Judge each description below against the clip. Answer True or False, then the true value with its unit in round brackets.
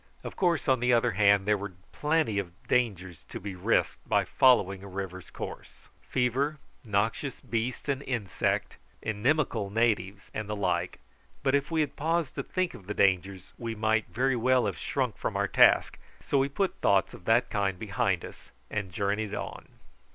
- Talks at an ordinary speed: True (180 wpm)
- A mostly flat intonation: False (4.7 semitones)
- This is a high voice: False (110 Hz)